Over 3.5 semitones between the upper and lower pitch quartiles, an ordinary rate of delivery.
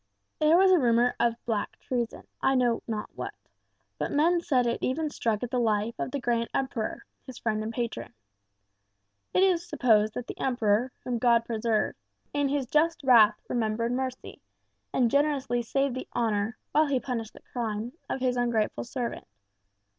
No: average, 2.8 semitones; average, 175 wpm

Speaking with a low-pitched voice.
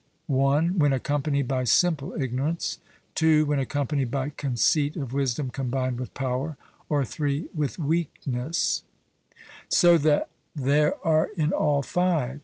No: medium, 145 Hz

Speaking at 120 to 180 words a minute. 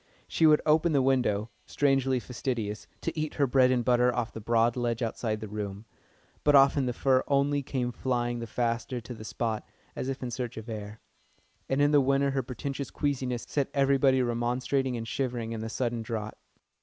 No: average, 195 wpm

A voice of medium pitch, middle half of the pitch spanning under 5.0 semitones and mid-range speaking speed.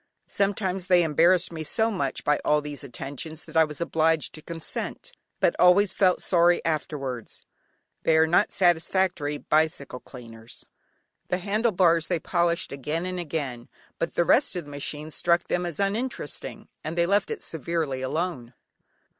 Yes: medium, 165 Hz; average, 3.4 semitones; average, 160 wpm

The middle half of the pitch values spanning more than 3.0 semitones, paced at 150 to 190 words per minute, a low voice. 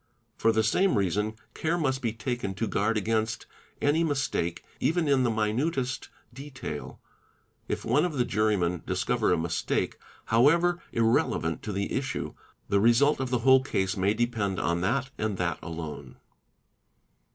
Yes: average, 5.0 semitones; average, 155 wpm; low, 115 Hz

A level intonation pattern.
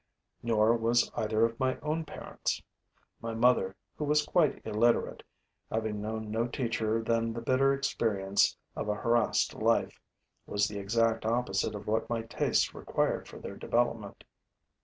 Yes: narrow, 1.8 semitones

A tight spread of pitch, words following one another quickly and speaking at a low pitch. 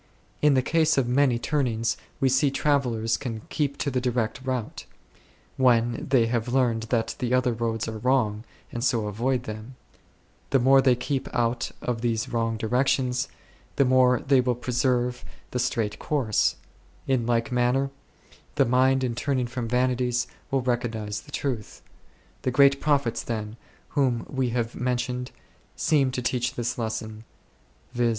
No: narrow, 2.2 semitones; average, 160 wpm; low, 125 Hz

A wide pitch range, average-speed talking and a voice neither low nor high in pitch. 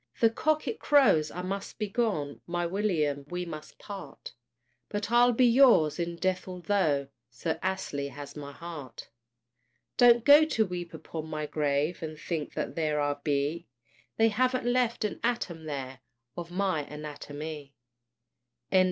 Yes: wide, 6.1 semitones; average, 155 wpm; medium, 170 Hz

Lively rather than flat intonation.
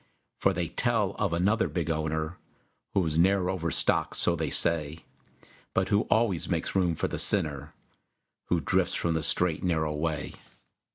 No: average, 3.3 semitones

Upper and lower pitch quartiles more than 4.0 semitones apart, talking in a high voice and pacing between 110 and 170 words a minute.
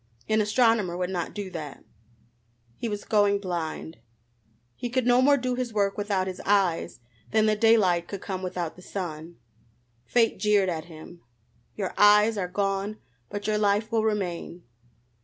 No: average, 3.2 semitones; high, 200 Hz; average, 160 wpm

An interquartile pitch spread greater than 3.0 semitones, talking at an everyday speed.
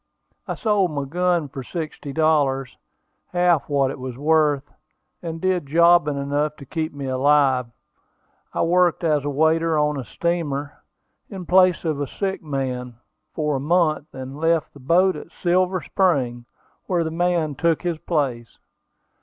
Yes: average, 3.7 semitones; average, 155 wpm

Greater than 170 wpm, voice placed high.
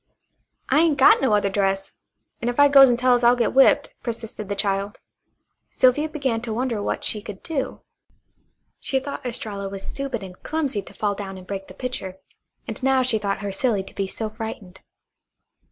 Yes: average, 190 wpm; high, 225 Hz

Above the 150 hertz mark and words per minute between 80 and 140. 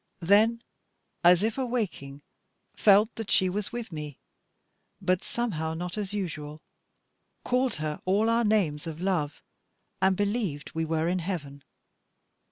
Yes: medium, 185 Hz; slow, 135 wpm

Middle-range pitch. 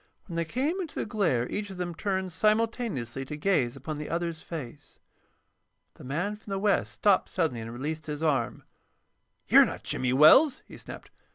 Yes: medium, 165 Hz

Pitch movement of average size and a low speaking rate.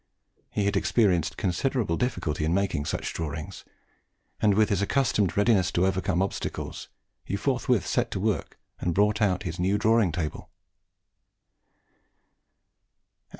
Yes: average, 3.6 semitones; slow, 130 wpm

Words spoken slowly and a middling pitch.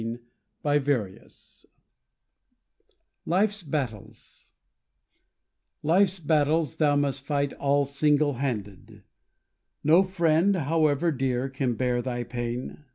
Yes: slow, 85 wpm; medium, 145 Hz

